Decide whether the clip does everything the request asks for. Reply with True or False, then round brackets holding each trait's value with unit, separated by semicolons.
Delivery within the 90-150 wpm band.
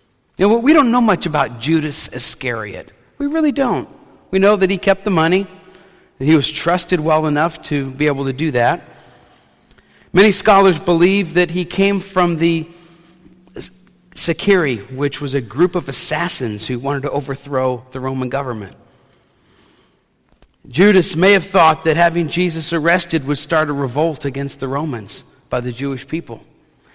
False (160 wpm)